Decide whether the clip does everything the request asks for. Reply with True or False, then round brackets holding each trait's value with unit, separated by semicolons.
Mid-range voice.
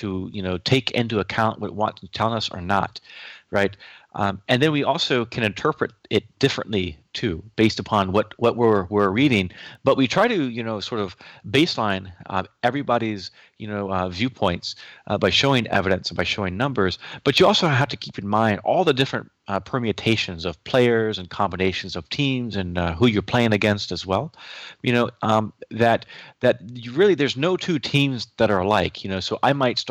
False (110 Hz)